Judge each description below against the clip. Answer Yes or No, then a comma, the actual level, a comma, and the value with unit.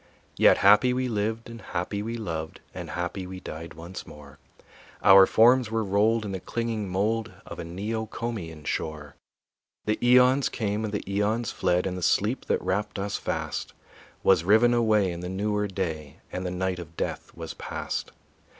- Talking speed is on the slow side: No, average, 175 wpm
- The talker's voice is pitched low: Yes, low, 100 Hz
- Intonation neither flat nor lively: Yes, average, 3.8 semitones